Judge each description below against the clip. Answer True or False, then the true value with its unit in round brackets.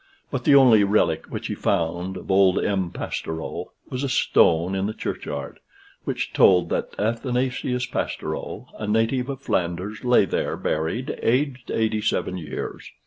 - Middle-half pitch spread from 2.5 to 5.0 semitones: False (5.4 semitones)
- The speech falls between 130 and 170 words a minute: True (145 wpm)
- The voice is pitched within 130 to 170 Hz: False (105 Hz)